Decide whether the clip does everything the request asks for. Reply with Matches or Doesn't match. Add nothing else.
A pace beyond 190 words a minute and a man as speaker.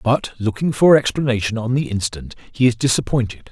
Doesn't match